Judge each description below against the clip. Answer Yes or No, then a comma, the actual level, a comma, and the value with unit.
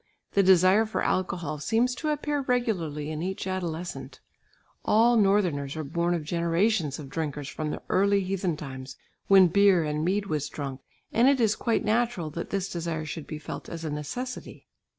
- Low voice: No, medium, 175 Hz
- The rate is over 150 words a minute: Yes, average, 175 wpm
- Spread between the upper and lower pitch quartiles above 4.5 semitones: Yes, average, 5.1 semitones